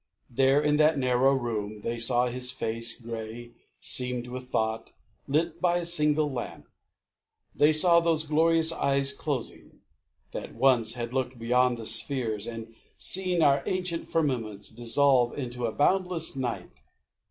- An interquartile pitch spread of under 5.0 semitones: Yes, average, 4.4 semitones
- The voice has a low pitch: Yes, low, 130 Hz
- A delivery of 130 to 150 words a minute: Yes, average, 140 wpm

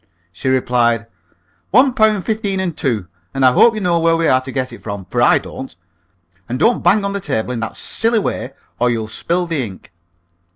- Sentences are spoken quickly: Yes, fast, 210 wpm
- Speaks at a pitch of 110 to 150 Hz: Yes, medium, 140 Hz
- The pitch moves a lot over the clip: Yes, wide, 8.7 semitones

